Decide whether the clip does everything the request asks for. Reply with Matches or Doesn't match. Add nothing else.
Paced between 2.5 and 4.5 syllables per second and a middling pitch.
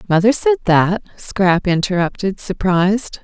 Doesn't match